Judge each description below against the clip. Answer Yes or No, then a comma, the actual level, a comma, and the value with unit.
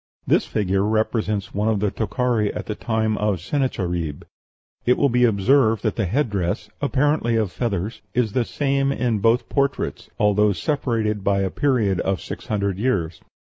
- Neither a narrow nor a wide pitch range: Yes, average, 3.8 semitones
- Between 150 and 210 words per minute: Yes, average, 170 wpm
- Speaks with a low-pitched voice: Yes, low, 110 Hz